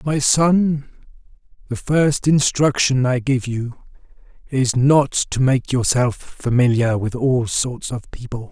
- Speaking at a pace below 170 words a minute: Yes, slow, 135 wpm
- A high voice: No, low, 130 Hz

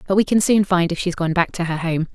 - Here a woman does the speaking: Yes, female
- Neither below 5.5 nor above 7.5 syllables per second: Yes, 6.1 syllables/s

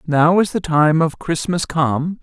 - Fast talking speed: No, average, 190 wpm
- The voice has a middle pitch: Yes, medium, 160 Hz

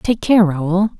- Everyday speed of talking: Yes, average, 180 wpm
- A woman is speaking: Yes, female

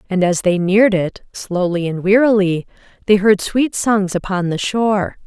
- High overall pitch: Yes, high, 195 Hz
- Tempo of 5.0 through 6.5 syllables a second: No, 4.6 syllables/s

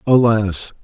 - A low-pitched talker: Yes, low, 105 Hz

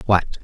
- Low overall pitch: Yes, very low, 95 Hz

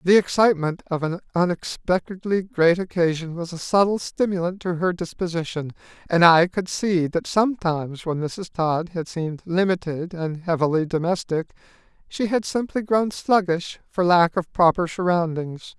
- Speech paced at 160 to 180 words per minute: No, average, 150 wpm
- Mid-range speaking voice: Yes, medium, 175 Hz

